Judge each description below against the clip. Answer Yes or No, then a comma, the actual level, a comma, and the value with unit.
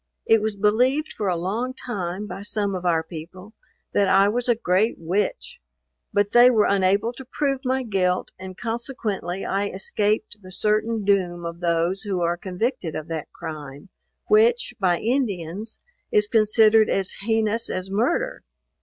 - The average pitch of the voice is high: Yes, high, 205 Hz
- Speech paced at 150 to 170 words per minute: Yes, average, 160 wpm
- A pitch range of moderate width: Yes, average, 3.7 semitones